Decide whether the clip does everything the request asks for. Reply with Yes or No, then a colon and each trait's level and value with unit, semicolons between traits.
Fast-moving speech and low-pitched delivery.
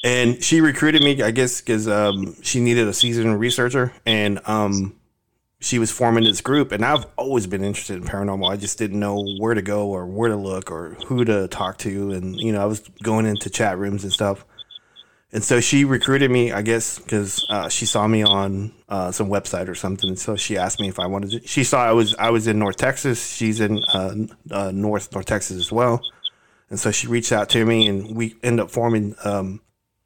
Yes: fast, 225 wpm; low, 110 Hz